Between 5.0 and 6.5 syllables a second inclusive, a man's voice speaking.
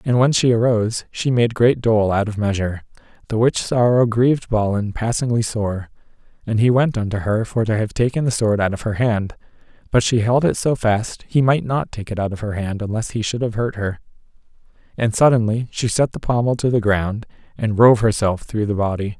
Yes: 5.3 syllables/s; male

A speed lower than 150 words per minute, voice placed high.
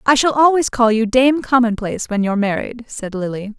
No: average, 200 wpm; high, 235 Hz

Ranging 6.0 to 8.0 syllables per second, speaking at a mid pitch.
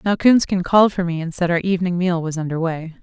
Yes: 6.3 syllables/s; medium, 175 Hz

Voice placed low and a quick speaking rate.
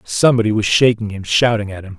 Yes: low, 110 Hz; fast, 210 wpm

